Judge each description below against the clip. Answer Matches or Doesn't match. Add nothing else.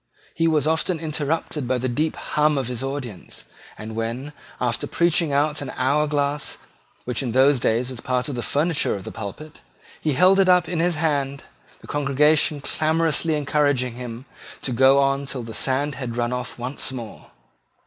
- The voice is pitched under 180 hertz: Matches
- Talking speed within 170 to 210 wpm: Matches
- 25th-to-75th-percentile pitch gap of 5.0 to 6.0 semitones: Doesn't match